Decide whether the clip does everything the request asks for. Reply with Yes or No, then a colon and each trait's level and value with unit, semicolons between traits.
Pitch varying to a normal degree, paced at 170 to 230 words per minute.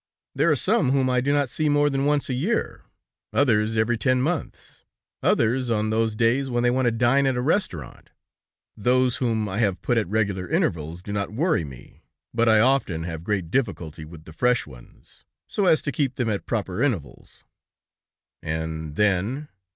No: wide, 5.9 semitones; average, 185 wpm